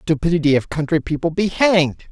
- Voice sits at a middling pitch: Yes, medium, 165 Hz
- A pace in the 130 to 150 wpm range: No, average, 170 wpm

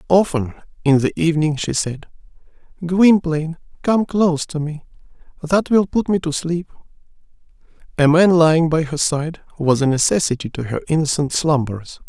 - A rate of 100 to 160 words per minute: Yes, average, 150 wpm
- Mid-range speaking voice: Yes, medium, 160 Hz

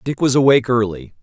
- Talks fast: No, average, 195 wpm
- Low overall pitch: Yes, low, 120 Hz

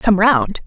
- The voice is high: Yes, high, 210 Hz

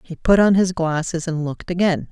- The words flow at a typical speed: No, fast, 225 wpm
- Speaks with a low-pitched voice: No, medium, 170 Hz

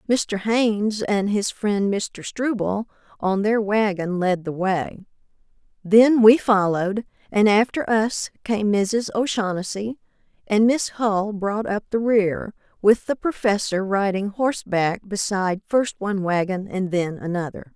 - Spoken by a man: No, female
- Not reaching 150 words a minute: Yes, average, 140 wpm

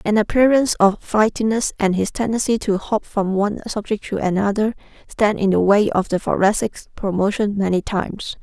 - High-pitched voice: Yes, high, 205 Hz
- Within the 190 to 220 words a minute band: No, average, 170 wpm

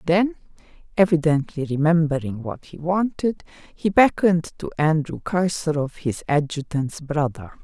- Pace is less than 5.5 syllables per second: Yes, 4.6 syllables/s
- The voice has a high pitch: No, medium, 160 Hz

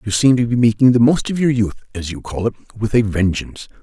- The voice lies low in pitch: Yes, low, 115 Hz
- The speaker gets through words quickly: Yes, fast, 265 wpm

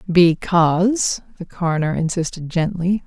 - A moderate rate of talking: No, slow, 100 wpm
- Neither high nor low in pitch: Yes, medium, 175 Hz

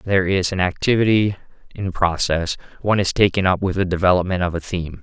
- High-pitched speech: No, very low, 95 Hz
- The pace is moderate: Yes, average, 190 wpm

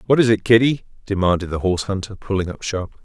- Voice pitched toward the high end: No, low, 100 Hz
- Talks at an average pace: No, fast, 215 wpm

